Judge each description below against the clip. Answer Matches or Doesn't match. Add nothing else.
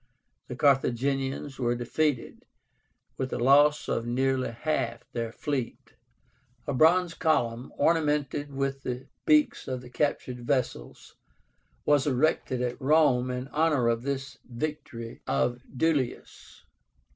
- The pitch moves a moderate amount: Matches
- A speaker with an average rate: Doesn't match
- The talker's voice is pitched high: Doesn't match